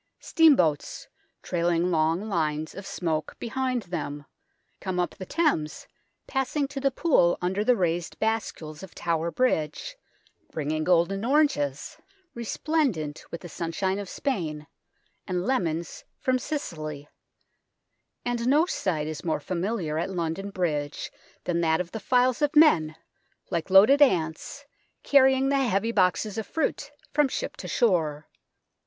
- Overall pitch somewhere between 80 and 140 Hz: No, medium, 185 Hz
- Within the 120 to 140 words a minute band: Yes, slow, 135 wpm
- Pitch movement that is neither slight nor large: No, wide, 8.0 semitones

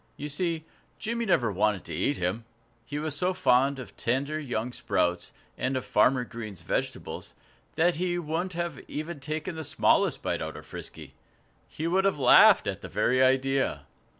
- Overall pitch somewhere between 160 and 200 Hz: No, medium, 145 Hz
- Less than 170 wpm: No, average, 175 wpm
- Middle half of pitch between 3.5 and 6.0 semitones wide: Yes, average, 5.2 semitones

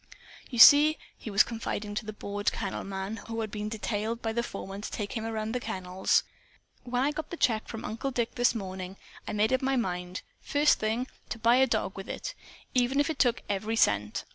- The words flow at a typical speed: No, fast, 215 wpm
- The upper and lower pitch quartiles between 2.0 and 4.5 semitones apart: Yes, average, 3.3 semitones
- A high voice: Yes, high, 220 Hz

